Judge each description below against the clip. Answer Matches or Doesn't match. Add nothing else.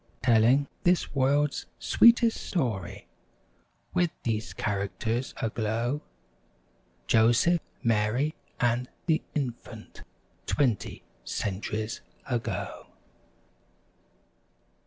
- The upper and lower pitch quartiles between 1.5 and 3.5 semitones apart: Doesn't match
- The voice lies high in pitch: Doesn't match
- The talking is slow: Matches